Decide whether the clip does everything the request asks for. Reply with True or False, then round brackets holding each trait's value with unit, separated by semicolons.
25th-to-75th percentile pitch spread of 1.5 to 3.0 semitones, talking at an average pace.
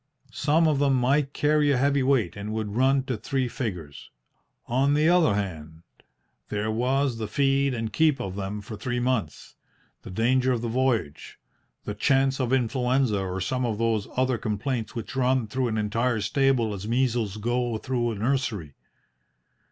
False (3.9 semitones; 170 wpm)